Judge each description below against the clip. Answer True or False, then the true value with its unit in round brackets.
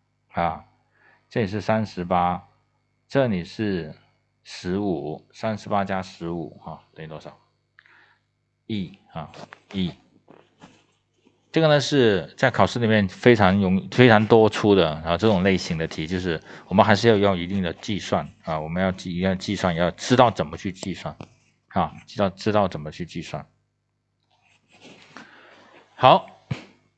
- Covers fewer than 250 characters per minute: True (210 characters per minute)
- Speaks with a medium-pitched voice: False (100 Hz)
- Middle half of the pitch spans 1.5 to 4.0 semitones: True (3.7 semitones)